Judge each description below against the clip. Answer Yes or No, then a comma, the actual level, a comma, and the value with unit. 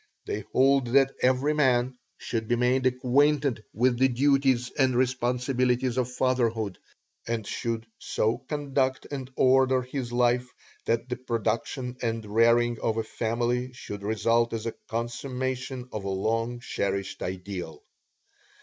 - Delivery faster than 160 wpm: No, slow, 135 wpm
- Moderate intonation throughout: No, narrow, 2.1 semitones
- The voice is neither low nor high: No, low, 125 Hz